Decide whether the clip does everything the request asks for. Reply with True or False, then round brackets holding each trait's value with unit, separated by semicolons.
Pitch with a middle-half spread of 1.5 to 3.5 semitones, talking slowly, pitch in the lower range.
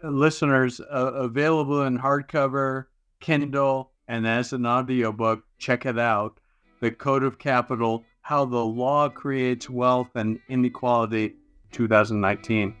True (2.9 semitones; 115 wpm; 125 Hz)